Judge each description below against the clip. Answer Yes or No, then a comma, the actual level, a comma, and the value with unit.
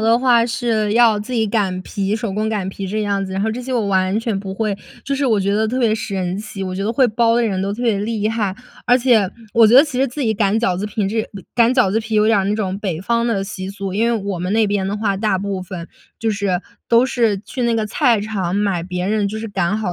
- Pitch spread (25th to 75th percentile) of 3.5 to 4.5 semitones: No, average, 2.8 semitones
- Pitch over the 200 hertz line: Yes, high, 210 Hz